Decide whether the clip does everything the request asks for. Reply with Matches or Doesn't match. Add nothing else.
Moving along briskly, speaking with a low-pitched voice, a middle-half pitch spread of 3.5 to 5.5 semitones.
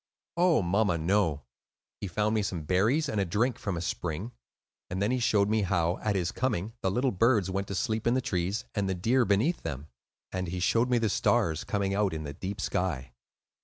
Matches